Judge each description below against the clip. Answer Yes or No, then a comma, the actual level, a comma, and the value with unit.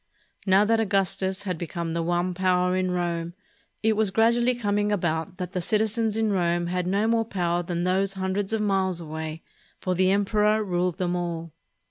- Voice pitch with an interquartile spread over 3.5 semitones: No, average, 2.9 semitones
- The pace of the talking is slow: No, average, 180 wpm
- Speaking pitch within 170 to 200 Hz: Yes, medium, 185 Hz